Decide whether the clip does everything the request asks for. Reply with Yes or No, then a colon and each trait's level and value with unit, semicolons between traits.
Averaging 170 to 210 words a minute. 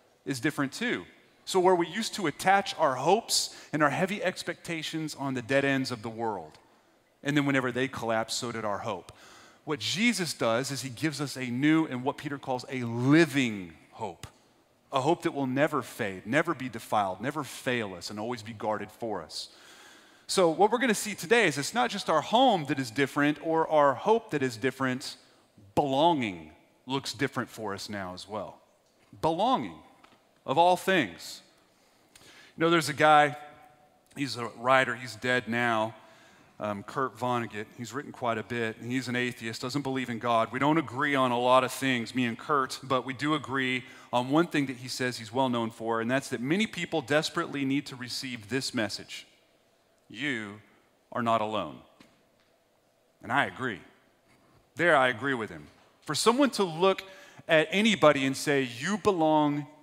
Yes: average, 185 wpm